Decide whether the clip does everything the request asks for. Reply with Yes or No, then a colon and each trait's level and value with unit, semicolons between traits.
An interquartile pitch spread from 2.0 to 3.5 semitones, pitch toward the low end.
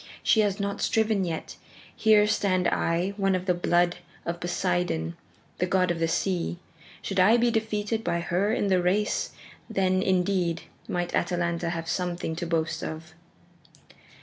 No: average, 2.7 semitones; medium, 180 Hz